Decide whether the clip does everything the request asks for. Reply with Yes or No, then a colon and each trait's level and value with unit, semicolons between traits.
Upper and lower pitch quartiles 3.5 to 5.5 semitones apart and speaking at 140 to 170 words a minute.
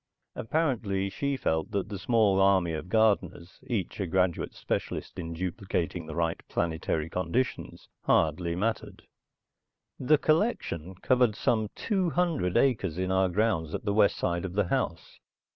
Yes: average, 4.8 semitones; average, 145 wpm